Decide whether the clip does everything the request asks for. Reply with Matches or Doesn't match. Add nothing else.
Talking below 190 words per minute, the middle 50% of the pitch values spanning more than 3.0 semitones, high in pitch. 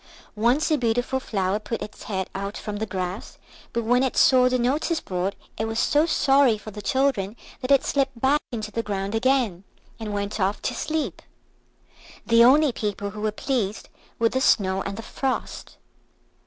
Matches